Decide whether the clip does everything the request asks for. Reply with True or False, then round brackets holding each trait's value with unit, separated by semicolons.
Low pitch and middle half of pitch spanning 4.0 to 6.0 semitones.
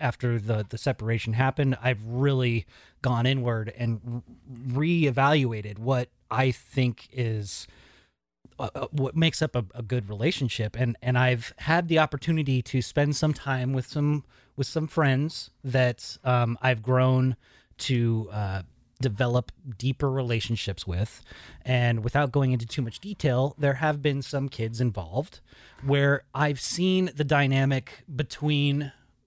False (130 Hz; 3.1 semitones)